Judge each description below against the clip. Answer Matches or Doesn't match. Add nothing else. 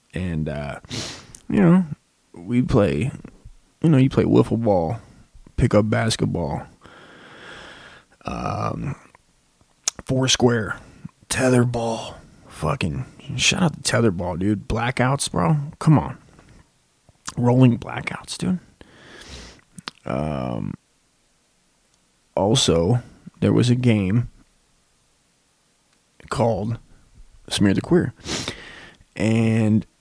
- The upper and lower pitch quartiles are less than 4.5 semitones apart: Doesn't match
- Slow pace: Matches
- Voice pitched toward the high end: Doesn't match